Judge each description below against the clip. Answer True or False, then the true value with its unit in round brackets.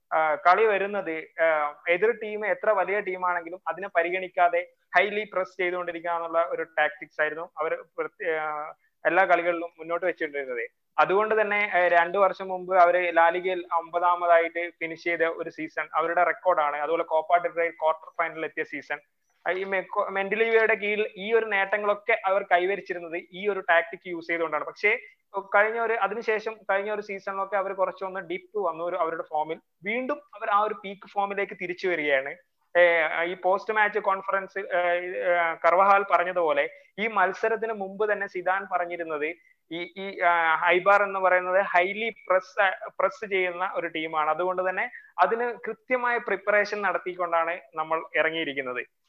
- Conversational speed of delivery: False (130 wpm)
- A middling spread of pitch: True (3.2 semitones)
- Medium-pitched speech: True (180 Hz)